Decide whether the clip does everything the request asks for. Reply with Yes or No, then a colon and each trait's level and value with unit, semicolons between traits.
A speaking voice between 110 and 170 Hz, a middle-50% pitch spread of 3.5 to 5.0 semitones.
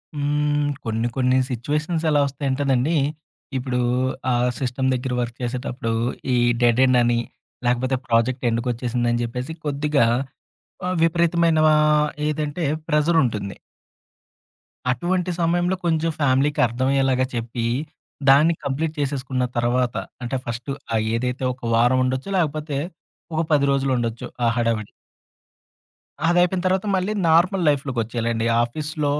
Yes: low, 135 Hz; average, 3.9 semitones